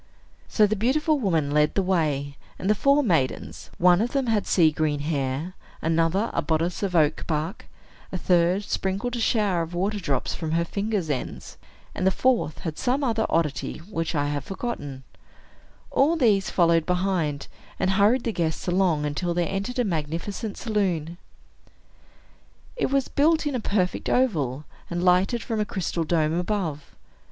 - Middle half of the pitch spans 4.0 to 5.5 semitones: Yes, average, 5.1 semitones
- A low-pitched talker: No, medium, 180 Hz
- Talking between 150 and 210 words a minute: Yes, average, 165 wpm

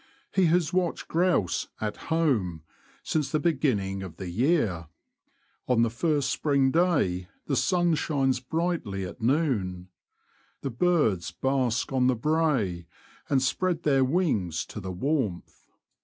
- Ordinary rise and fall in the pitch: No, wide, 8.6 semitones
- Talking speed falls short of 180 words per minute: Yes, average, 140 wpm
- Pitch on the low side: Yes, low, 130 Hz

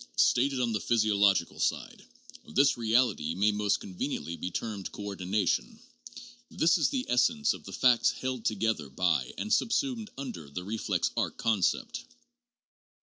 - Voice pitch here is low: Yes, low, 110 Hz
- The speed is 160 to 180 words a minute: No, average, 145 wpm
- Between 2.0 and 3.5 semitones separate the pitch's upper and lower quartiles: No, average, 5.2 semitones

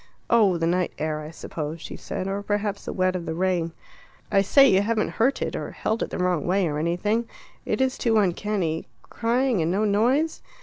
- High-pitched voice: Yes, high, 195 Hz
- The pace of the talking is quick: Yes, fast, 210 wpm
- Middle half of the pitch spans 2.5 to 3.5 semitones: No, average, 4.6 semitones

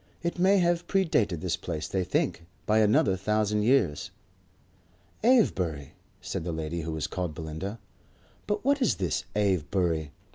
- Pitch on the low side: Yes, very low, 95 Hz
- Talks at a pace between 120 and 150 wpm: Yes, average, 145 wpm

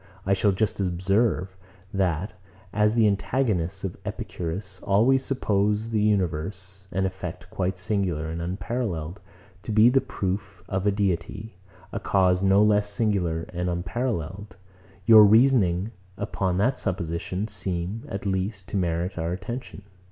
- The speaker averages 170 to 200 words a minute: No, slow, 135 wpm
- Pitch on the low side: Yes, very low, 95 Hz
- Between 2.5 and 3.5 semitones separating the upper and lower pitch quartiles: Yes, average, 2.8 semitones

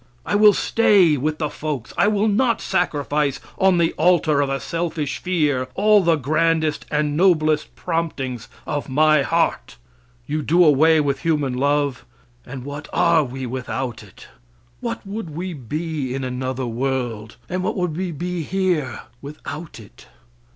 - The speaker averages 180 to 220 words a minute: No, average, 155 wpm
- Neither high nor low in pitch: Yes, medium, 155 Hz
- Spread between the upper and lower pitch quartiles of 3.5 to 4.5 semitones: Yes, average, 4.1 semitones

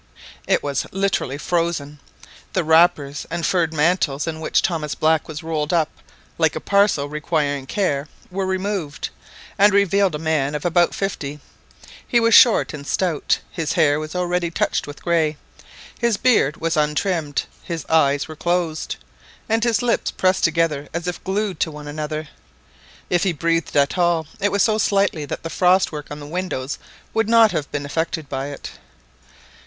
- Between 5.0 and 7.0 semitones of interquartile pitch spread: No, average, 3.8 semitones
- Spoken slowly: No, average, 170 wpm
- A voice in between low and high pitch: Yes, medium, 165 Hz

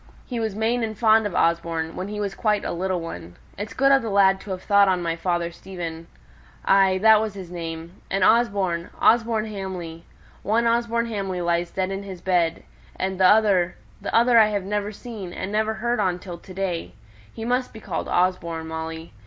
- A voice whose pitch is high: Yes, high, 195 Hz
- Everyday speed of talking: Yes, average, 195 wpm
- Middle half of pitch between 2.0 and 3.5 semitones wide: No, average, 4.0 semitones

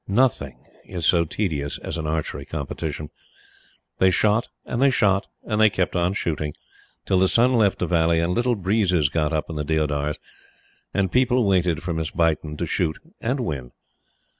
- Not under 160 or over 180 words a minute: Yes, average, 175 wpm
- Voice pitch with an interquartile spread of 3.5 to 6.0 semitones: Yes, average, 4.9 semitones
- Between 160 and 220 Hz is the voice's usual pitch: No, very low, 85 Hz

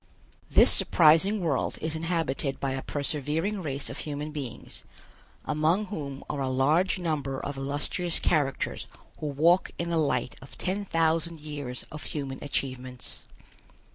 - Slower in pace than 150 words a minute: Yes, average, 140 wpm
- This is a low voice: No, medium, 150 Hz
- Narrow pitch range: No, average, 3.3 semitones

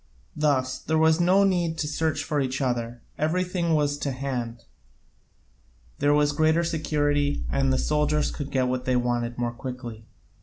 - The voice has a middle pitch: Yes, medium, 145 Hz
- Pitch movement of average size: Yes, average, 3.7 semitones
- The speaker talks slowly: No, average, 160 wpm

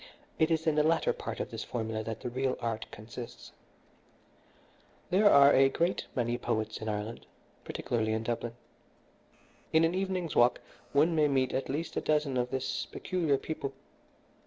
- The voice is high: No, low, 135 Hz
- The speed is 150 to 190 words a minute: Yes, average, 165 wpm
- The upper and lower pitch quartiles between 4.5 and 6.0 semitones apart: Yes, average, 5.2 semitones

